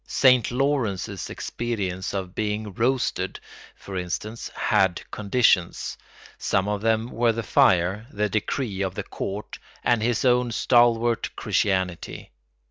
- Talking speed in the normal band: No, slow, 125 wpm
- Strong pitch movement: No, average, 3.7 semitones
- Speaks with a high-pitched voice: No, low, 110 Hz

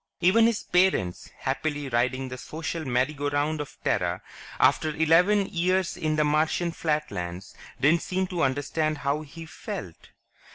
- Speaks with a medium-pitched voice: Yes, medium, 155 Hz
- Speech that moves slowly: No, average, 150 wpm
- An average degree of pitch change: Yes, average, 3.5 semitones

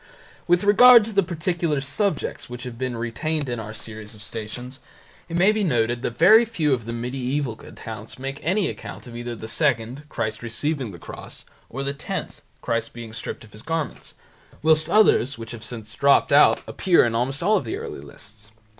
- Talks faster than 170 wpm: Yes, average, 190 wpm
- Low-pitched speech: Yes, low, 130 Hz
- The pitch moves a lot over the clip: Yes, wide, 5.7 semitones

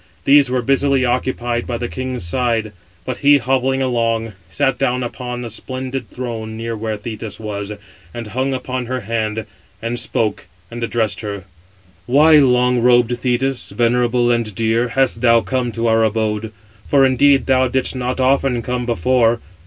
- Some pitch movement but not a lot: No, narrow, 2.1 semitones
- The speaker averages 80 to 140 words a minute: No, average, 165 wpm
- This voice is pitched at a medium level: No, low, 120 Hz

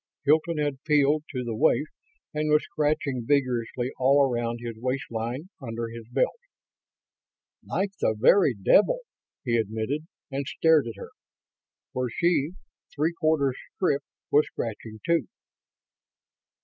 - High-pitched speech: No, low, 135 Hz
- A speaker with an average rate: No, slow, 125 wpm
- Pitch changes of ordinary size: Yes, average, 4.5 semitones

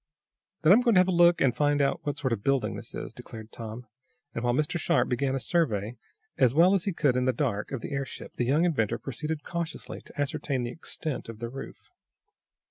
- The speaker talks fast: Yes, fast, 230 wpm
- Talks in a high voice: No, medium, 140 Hz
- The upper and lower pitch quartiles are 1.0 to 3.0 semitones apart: No, average, 4.9 semitones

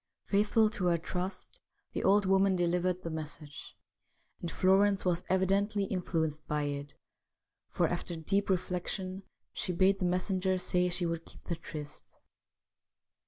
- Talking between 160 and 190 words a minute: No, average, 145 wpm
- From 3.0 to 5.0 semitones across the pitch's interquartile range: No, narrow, 2.4 semitones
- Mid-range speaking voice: Yes, medium, 180 Hz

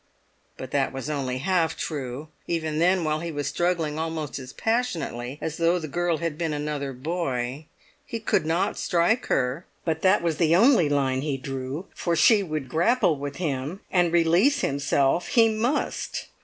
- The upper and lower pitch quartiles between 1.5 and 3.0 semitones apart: No, average, 3.8 semitones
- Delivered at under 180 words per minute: Yes, average, 170 wpm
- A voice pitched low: No, medium, 160 Hz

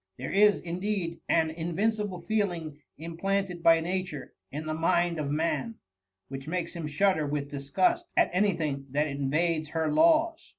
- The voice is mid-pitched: Yes, medium, 170 Hz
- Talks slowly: No, average, 160 wpm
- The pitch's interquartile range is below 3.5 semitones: No, average, 4.3 semitones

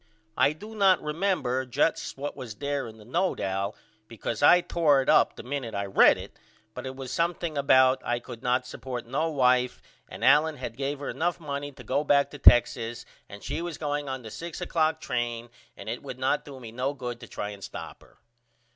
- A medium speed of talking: No, fast, 215 wpm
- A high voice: No, low, 135 Hz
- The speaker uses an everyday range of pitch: Yes, average, 3.8 semitones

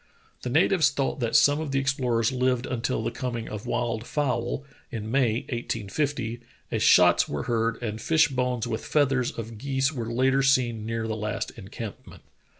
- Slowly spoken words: No, average, 170 wpm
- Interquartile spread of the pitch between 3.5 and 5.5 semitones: No, average, 2.9 semitones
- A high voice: No, low, 120 Hz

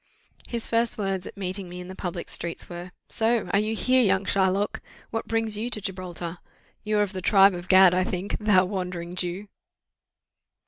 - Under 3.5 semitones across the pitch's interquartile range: Yes, average, 2.7 semitones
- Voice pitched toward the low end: No, high, 190 Hz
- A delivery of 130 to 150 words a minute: No, average, 190 wpm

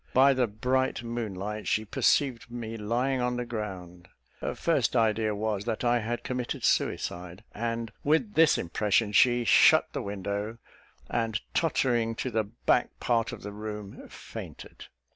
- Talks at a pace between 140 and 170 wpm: Yes, average, 155 wpm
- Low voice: Yes, low, 115 Hz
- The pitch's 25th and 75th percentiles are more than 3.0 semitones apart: No, average, 2.7 semitones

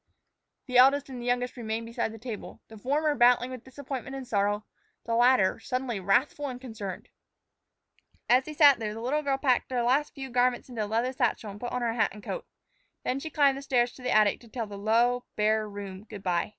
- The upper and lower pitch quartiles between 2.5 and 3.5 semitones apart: Yes, average, 3.2 semitones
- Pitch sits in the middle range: No, high, 245 Hz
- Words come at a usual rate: No, fast, 220 wpm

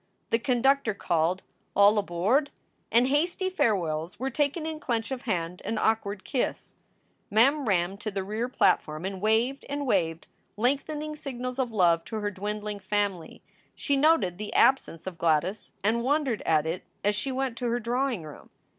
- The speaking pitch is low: No, high, 220 Hz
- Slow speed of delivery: No, average, 165 wpm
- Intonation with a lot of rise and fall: Yes, wide, 5.9 semitones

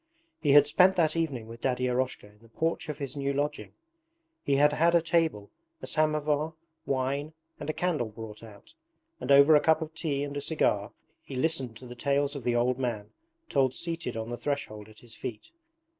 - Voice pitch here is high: No, medium, 140 Hz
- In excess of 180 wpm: Yes, average, 200 wpm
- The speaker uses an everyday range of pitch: Yes, average, 4.3 semitones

